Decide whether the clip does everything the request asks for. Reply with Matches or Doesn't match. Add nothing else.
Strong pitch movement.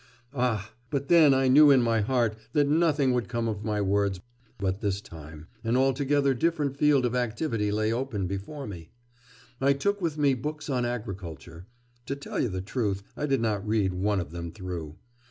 Matches